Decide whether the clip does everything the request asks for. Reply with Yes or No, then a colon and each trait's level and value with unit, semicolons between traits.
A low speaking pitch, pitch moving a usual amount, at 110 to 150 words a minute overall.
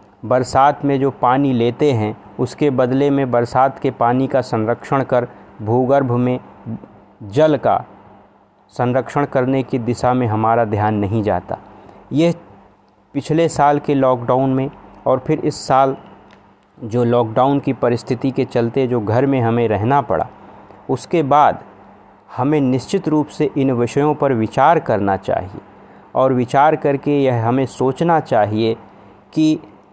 Yes: low, 130 Hz; average, 3.0 semitones; average, 140 wpm